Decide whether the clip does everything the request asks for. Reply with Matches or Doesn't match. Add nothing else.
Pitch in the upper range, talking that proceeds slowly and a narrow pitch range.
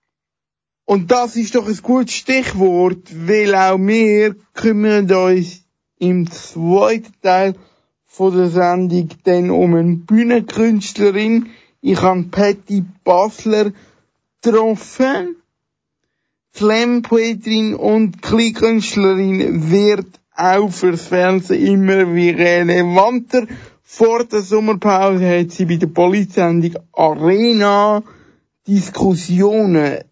Doesn't match